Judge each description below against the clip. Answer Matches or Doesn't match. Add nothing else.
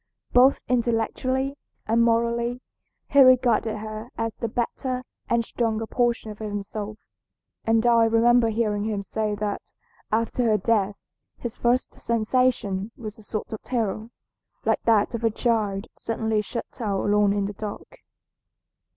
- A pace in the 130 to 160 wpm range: Matches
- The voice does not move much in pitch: Matches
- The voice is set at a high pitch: Matches